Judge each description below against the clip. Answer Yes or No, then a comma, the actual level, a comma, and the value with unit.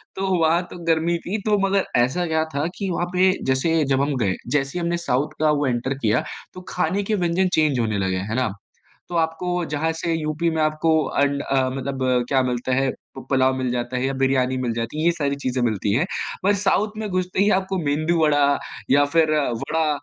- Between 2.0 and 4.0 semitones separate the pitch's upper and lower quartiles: No, average, 4.5 semitones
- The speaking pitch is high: No, medium, 150 Hz